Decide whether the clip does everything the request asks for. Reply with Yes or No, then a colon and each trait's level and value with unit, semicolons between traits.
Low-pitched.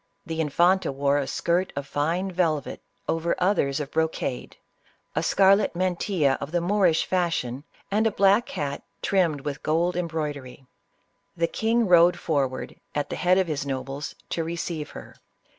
No: medium, 165 Hz